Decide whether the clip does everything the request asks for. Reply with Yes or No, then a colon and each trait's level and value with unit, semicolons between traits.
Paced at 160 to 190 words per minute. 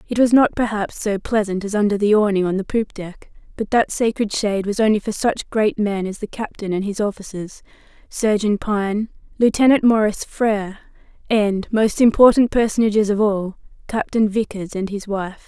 Yes: average, 180 wpm